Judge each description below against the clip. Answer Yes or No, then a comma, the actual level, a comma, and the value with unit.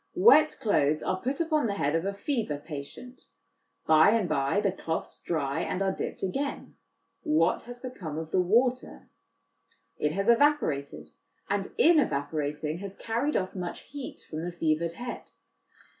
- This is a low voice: No, medium, 185 Hz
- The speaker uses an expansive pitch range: Yes, wide, 7.8 semitones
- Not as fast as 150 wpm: No, average, 160 wpm